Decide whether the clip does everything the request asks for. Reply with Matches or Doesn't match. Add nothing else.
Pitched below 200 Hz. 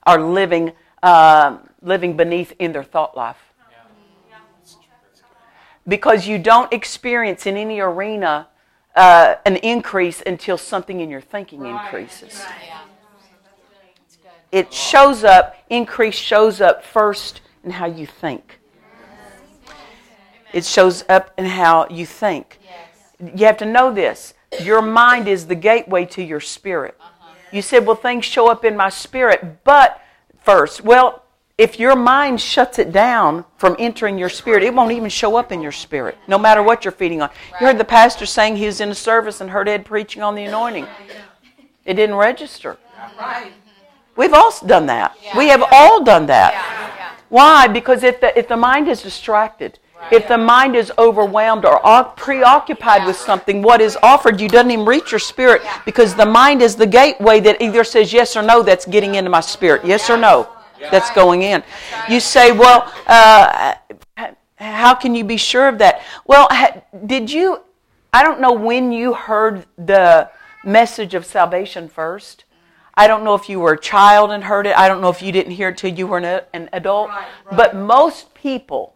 Doesn't match